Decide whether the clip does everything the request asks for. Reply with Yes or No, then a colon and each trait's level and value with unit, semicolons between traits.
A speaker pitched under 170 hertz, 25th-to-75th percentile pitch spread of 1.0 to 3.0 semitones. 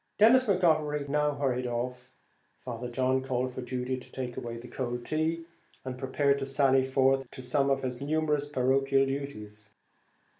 Yes: low, 135 Hz; narrow, 2.4 semitones